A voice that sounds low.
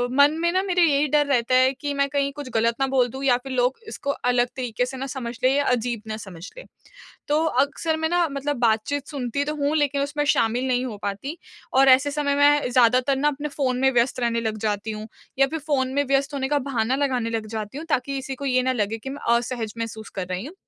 No: very high, 265 Hz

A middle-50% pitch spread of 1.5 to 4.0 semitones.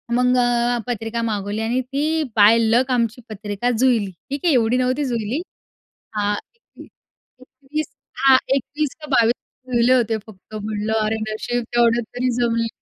Yes: narrow, 2.5 semitones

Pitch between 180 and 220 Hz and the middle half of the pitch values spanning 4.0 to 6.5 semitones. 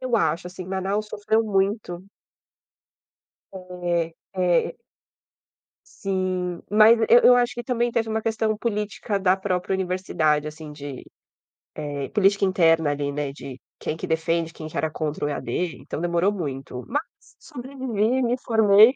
Yes: medium, 185 Hz; average, 5.1 semitones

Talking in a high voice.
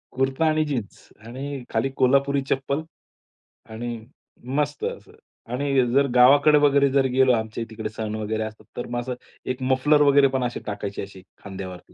No: low, 130 Hz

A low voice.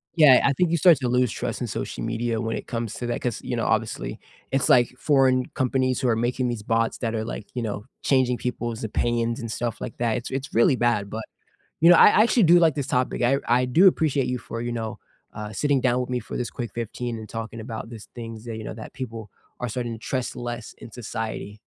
Yes: low, 120 Hz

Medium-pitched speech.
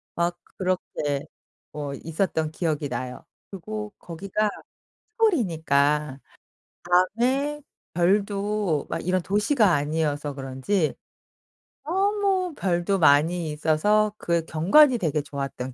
Yes: medium, 175 Hz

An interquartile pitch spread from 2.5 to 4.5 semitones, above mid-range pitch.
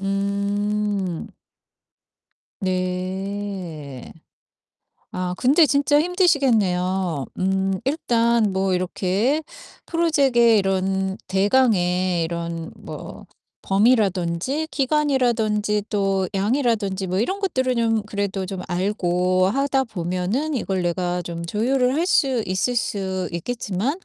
No: average, 5.1 semitones; high, 200 Hz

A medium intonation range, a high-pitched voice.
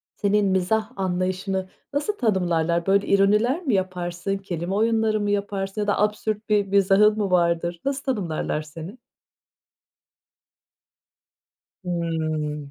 Yes: average, 3.3 semitones; high, 195 Hz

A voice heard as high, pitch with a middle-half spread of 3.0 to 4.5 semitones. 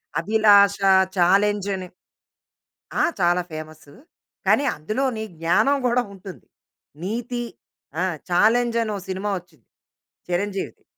Yes: high, 200 Hz; average, 3.7 semitones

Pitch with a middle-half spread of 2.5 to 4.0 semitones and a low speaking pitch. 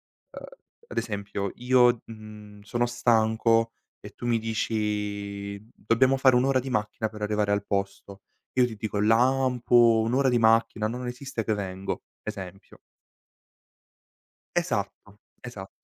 Yes: average, 2.9 semitones; low, 110 Hz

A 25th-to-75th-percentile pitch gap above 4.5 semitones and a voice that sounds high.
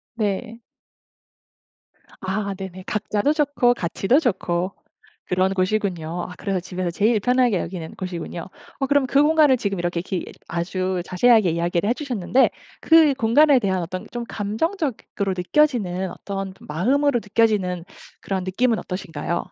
Yes: average, 5.2 semitones; high, 200 Hz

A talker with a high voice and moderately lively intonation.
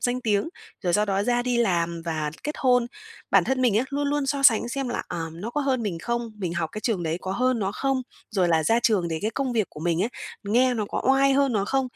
No: high, 230 Hz; wide, 5.8 semitones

